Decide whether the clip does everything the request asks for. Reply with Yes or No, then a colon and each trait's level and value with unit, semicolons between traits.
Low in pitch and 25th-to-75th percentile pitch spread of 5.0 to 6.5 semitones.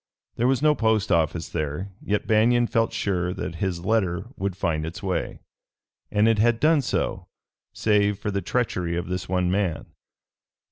No: low, 100 Hz; average, 4.2 semitones